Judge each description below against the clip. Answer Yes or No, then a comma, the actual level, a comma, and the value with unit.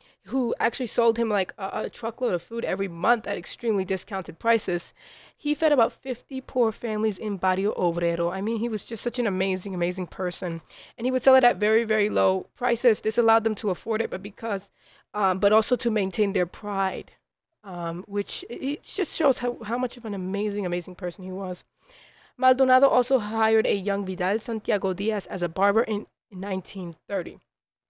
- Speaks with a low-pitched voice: No, high, 210 Hz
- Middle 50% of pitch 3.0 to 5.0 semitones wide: Yes, average, 3.8 semitones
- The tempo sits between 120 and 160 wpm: No, average, 190 wpm